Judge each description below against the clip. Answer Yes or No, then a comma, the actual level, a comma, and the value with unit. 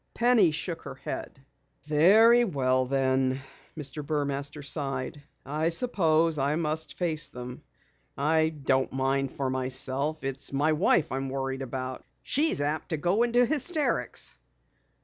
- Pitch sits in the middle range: Yes, medium, 145 Hz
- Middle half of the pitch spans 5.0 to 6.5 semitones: No, average, 3.6 semitones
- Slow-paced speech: Yes, slow, 130 wpm